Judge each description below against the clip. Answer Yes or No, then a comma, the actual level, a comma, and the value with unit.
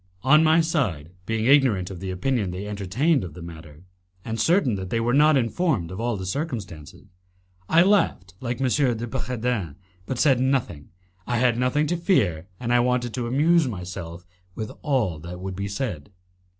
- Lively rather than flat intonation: Yes, wide, 6.5 semitones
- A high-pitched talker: No, low, 115 Hz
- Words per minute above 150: Yes, average, 180 wpm